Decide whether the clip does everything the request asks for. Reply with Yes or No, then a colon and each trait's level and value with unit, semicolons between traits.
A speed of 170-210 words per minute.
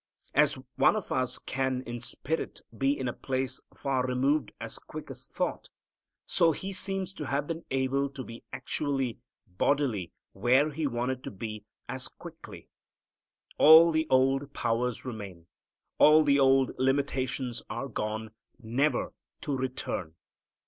No: average, 140 wpm